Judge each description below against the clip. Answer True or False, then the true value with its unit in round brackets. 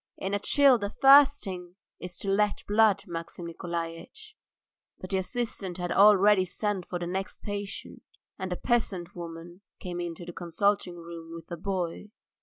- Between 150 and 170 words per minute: True (165 wpm)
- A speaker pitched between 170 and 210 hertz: True (185 Hz)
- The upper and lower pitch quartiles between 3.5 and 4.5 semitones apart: False (3.0 semitones)